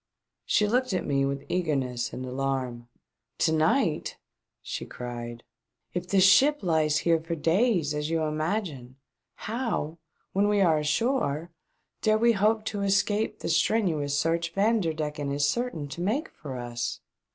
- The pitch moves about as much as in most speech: No, wide, 6.4 semitones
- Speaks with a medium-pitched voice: Yes, medium, 165 Hz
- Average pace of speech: Yes, average, 150 wpm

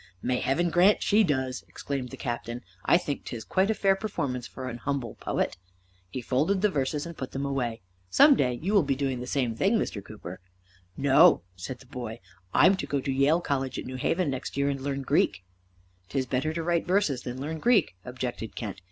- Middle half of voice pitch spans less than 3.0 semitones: No, average, 4.9 semitones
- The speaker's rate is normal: No, fast, 210 wpm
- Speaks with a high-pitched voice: No, low, 135 Hz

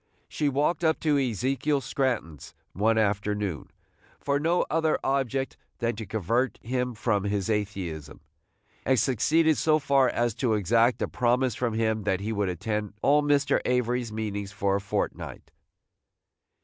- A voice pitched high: No, low, 120 Hz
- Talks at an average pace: Yes, average, 150 wpm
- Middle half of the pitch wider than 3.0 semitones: Yes, average, 4.8 semitones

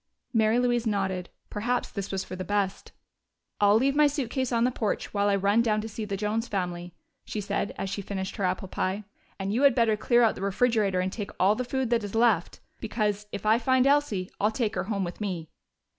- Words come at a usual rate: No, fast, 225 wpm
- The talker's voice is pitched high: Yes, high, 210 Hz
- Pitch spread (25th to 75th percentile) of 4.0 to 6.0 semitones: No, average, 3.3 semitones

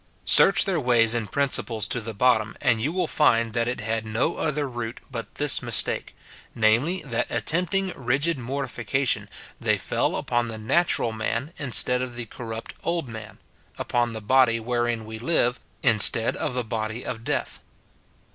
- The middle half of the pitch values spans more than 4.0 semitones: No, average, 3.4 semitones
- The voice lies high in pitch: No, low, 120 Hz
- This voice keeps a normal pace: Yes, average, 165 wpm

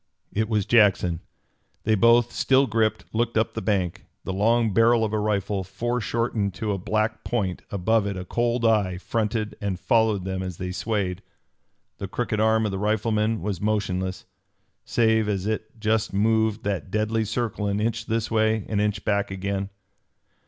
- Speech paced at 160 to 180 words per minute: Yes, average, 170 wpm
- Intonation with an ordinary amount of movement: No, narrow, 2.1 semitones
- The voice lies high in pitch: No, low, 110 Hz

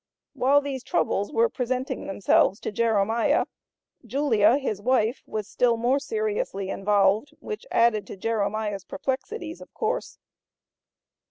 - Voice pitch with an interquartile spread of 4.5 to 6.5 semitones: Yes, average, 5.3 semitones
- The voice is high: Yes, high, 235 Hz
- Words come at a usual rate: No, slow, 120 wpm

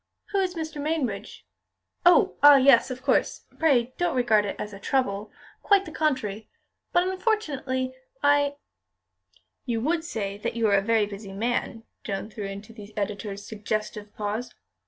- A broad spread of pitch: Yes, wide, 5.8 semitones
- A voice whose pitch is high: Yes, high, 235 Hz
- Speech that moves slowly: No, average, 155 wpm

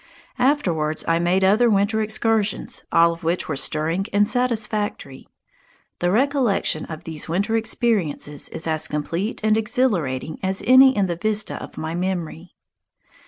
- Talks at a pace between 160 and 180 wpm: No, average, 145 wpm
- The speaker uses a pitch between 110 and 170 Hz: No, high, 190 Hz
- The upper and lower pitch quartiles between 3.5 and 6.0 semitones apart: Yes, average, 5.1 semitones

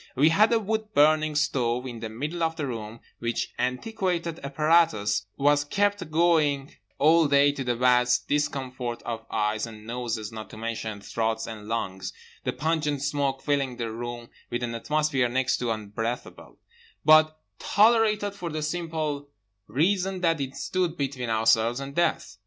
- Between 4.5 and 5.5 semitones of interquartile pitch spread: Yes, average, 5.2 semitones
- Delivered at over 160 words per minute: No, average, 155 wpm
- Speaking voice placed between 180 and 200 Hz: No, medium, 140 Hz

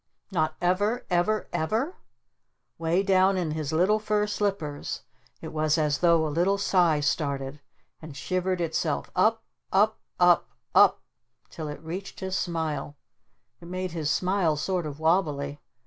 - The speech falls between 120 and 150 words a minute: Yes, average, 145 wpm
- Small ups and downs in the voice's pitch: No, average, 3.7 semitones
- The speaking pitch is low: No, medium, 175 Hz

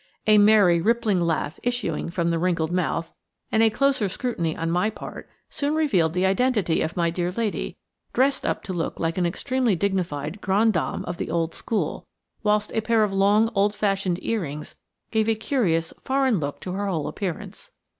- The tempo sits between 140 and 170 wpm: No, average, 185 wpm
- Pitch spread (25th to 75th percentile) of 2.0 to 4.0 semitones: No, average, 4.7 semitones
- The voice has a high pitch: Yes, high, 195 Hz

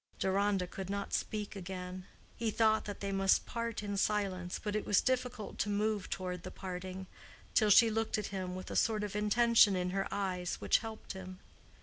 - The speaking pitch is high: Yes, high, 200 Hz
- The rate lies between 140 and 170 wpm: No, average, 195 wpm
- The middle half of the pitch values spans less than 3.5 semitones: Yes, narrow, 2.4 semitones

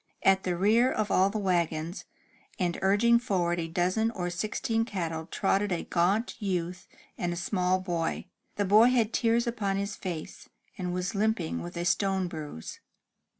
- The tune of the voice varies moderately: Yes, average, 3.4 semitones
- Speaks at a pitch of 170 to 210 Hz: Yes, high, 190 Hz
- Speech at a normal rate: Yes, average, 165 wpm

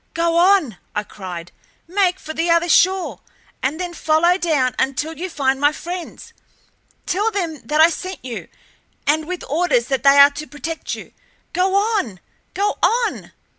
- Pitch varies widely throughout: No, average, 4.5 semitones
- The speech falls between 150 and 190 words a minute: Yes, average, 165 wpm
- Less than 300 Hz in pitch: No, very high, 325 Hz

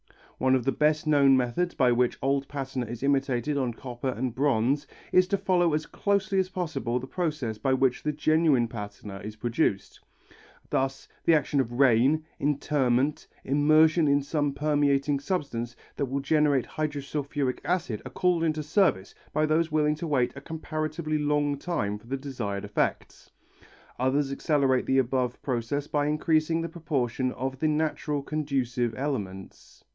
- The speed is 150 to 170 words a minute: Yes, average, 160 wpm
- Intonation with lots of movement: No, average, 3.4 semitones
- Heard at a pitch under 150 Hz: Yes, medium, 140 Hz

